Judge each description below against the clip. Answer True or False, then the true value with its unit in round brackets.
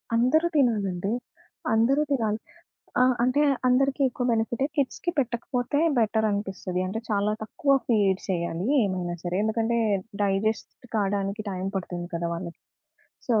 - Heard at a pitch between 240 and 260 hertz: False (215 Hz)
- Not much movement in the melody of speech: False (4.4 semitones)